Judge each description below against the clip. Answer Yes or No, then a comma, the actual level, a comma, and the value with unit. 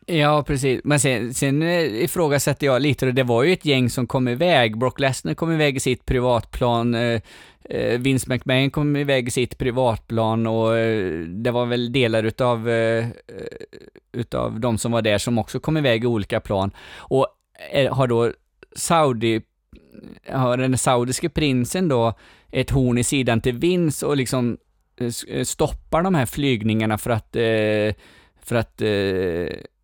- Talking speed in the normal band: Yes, average, 145 wpm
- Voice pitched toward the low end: Yes, low, 125 Hz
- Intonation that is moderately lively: Yes, average, 3.4 semitones